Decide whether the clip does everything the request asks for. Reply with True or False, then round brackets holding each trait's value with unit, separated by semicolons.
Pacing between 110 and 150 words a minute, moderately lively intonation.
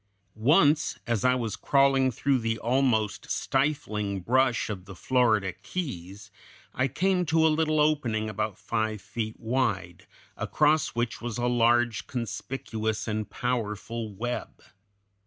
True (140 wpm; 3.8 semitones)